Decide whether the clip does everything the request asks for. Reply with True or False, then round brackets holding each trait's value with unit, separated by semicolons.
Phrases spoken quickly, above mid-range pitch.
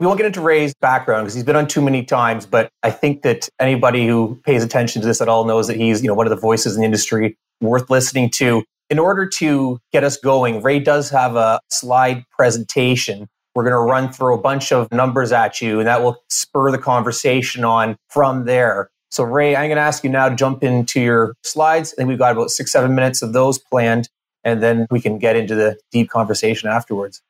False (230 wpm; 125 Hz)